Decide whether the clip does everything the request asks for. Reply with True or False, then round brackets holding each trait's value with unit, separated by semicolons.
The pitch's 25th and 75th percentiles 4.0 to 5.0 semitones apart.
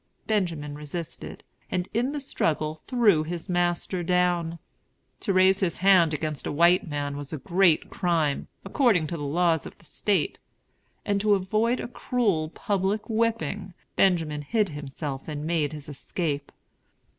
True (4.3 semitones)